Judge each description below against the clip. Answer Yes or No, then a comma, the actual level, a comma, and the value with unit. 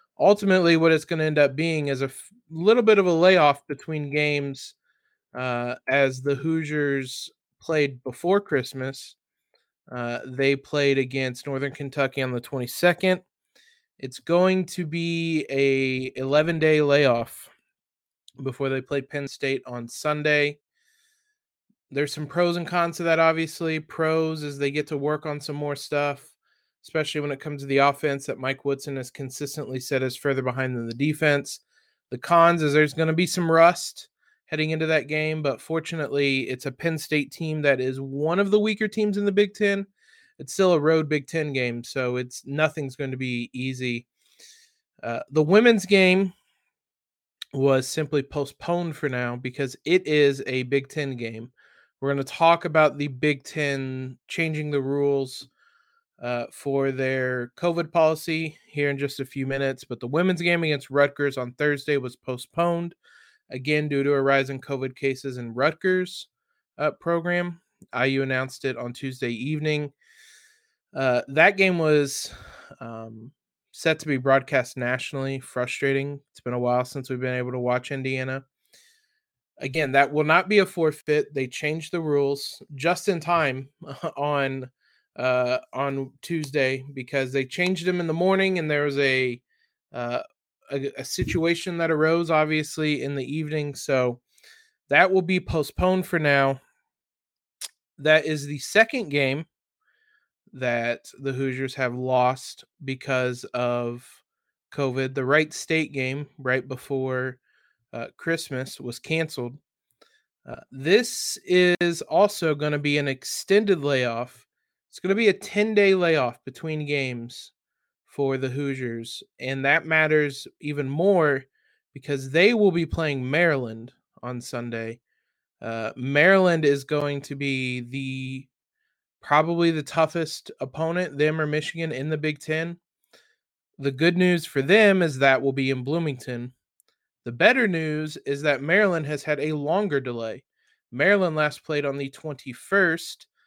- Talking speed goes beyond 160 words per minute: No, average, 155 wpm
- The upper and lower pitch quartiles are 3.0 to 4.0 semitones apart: Yes, average, 3.7 semitones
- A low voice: No, medium, 145 Hz